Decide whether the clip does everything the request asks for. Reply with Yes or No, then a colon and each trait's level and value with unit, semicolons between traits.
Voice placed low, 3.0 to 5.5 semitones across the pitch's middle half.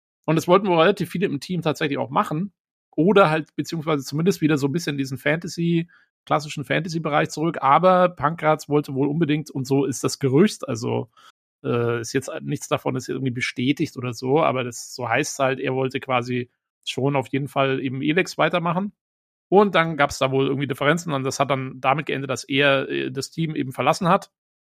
No: medium, 145 Hz; average, 3.6 semitones